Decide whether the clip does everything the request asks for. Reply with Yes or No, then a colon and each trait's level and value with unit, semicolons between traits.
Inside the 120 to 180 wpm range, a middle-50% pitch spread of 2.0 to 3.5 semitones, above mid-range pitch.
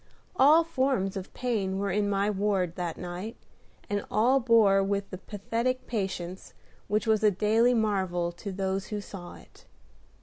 Yes: average, 160 wpm; average, 3.0 semitones; high, 205 Hz